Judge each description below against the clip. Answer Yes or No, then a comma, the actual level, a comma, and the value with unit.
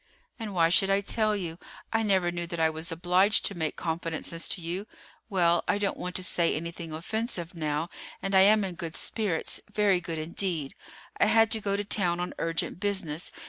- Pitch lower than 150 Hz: No, medium, 180 Hz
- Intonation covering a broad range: No, average, 3.3 semitones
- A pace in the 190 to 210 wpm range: Yes, average, 200 wpm